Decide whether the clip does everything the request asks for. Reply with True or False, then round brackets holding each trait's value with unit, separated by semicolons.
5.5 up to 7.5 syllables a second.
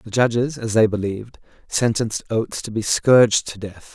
False (5.3 syllables/s)